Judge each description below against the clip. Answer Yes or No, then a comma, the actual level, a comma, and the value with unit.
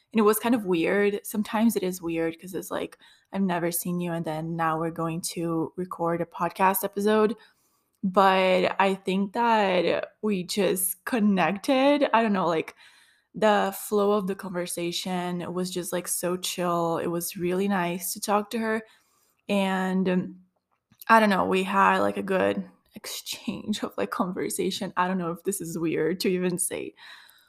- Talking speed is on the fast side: No, average, 175 wpm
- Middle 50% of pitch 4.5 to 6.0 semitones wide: No, average, 3.4 semitones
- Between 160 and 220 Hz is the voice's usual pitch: Yes, medium, 185 Hz